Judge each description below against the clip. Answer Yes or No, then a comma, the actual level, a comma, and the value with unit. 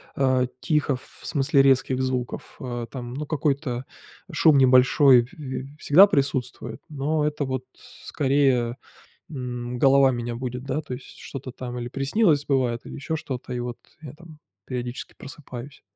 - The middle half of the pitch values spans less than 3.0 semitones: Yes, narrow, 2.4 semitones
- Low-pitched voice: Yes, low, 130 Hz